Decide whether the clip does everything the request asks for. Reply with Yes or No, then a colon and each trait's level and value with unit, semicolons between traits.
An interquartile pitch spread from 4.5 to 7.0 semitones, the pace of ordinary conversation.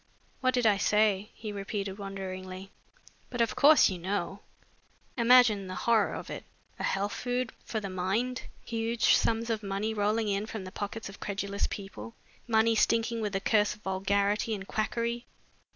No: narrow, 2.6 semitones; average, 170 wpm